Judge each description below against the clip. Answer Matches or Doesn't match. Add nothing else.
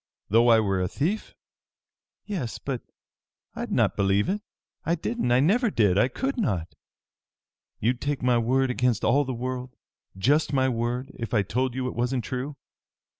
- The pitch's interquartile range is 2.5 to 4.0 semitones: Matches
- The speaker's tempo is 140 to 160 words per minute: Doesn't match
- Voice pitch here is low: Matches